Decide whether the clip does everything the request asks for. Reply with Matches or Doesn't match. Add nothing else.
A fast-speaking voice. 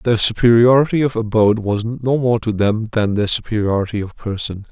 Doesn't match